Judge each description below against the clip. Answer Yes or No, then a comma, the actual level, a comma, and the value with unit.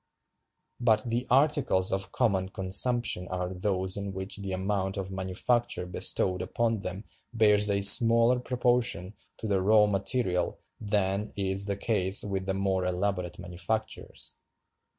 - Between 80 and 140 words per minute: Yes, slow, 135 wpm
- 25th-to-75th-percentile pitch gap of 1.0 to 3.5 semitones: Yes, average, 2.9 semitones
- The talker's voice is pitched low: Yes, low, 100 Hz